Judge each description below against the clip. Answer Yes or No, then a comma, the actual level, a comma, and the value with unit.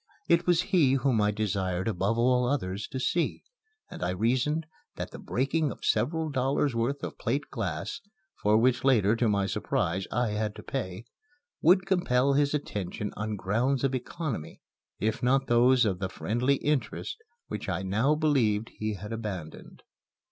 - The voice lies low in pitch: Yes, low, 120 Hz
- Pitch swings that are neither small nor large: Yes, average, 4.9 semitones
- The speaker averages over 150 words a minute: Yes, average, 165 wpm